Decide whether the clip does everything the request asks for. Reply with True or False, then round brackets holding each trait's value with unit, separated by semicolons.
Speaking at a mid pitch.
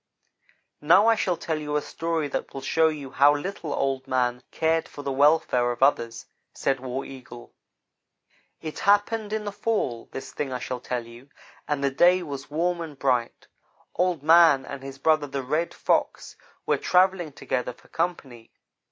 True (145 Hz)